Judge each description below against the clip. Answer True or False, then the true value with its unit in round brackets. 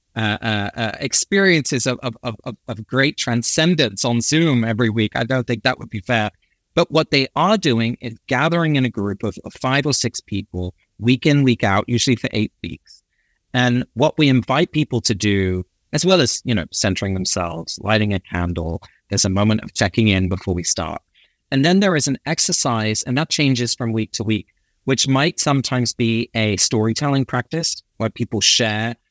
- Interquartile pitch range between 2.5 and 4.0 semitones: False (4.4 semitones)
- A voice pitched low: True (120 Hz)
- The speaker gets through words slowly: False (195 wpm)